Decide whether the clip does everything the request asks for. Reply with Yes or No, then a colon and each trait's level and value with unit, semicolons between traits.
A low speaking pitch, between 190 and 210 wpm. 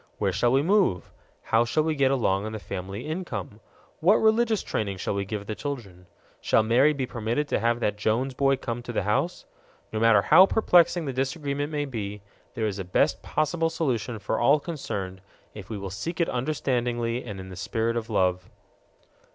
Yes: low, 120 Hz; average, 195 wpm